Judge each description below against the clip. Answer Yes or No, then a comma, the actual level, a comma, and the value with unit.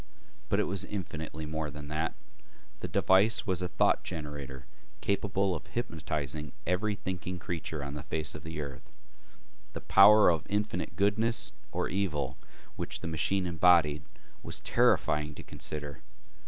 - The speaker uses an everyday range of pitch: Yes, average, 4.4 semitones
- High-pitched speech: No, very low, 80 Hz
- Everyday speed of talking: Yes, average, 145 wpm